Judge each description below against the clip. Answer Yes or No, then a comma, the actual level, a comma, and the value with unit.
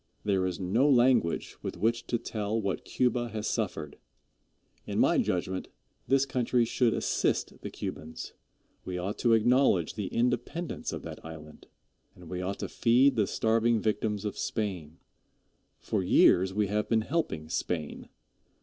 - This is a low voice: Yes, low, 105 Hz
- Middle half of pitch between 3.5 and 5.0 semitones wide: Yes, average, 4.6 semitones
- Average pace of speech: Yes, average, 150 wpm